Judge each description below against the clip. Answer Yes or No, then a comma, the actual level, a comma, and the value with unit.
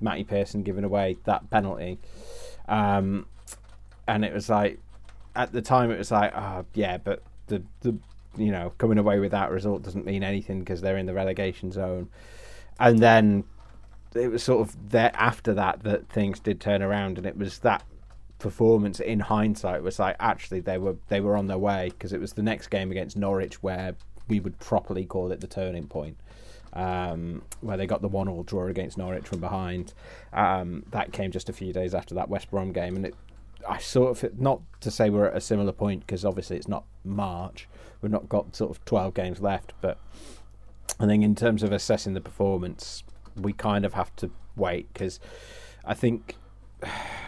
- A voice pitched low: Yes, low, 100 Hz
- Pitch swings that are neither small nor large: No, narrow, 2.0 semitones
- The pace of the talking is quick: No, average, 195 wpm